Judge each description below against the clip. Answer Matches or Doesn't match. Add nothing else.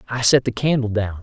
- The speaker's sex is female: Doesn't match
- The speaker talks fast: Matches